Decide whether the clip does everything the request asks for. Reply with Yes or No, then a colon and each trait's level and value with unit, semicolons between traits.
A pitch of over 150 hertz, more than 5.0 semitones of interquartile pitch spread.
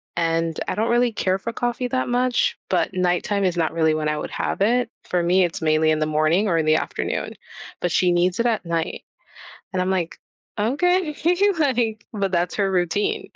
Yes: medium, 185 Hz; wide, 5.6 semitones